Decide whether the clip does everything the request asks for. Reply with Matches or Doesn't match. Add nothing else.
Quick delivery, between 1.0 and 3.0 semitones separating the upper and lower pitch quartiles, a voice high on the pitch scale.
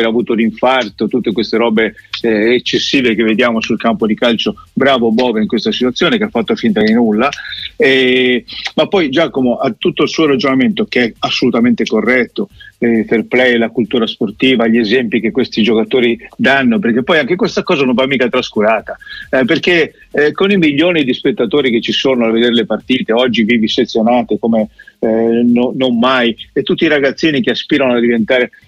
Doesn't match